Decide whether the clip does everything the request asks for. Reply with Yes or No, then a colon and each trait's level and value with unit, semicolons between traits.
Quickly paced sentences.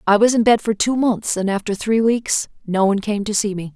Yes: fast, 270 wpm